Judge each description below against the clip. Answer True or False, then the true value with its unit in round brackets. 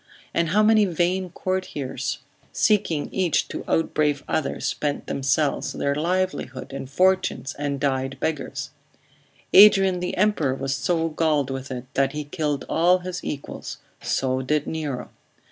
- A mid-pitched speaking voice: True (150 Hz)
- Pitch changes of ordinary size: True (4.8 semitones)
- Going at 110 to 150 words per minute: True (140 wpm)